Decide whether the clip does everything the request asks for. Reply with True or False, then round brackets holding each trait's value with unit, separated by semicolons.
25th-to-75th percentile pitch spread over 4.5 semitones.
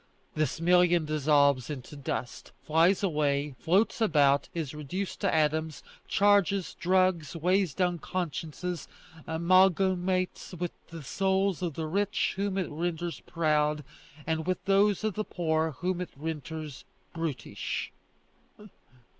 False (3.4 semitones)